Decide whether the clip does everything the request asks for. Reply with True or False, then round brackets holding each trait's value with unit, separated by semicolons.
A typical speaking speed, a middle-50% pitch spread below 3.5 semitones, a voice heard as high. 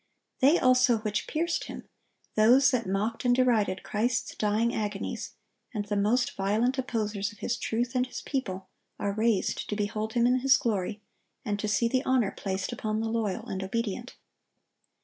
True (170 wpm; 3.1 semitones; 225 Hz)